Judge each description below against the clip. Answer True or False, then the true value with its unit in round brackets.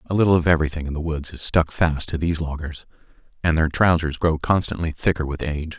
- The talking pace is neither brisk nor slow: False (220 wpm)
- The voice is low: True (80 Hz)